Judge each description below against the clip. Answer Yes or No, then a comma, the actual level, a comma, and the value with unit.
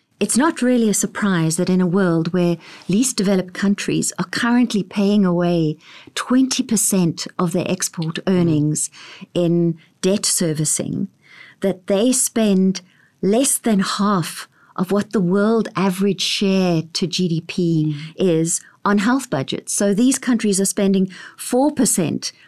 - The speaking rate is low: Yes, slow, 130 wpm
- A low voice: No, high, 195 Hz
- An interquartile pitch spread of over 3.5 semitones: No, average, 3.1 semitones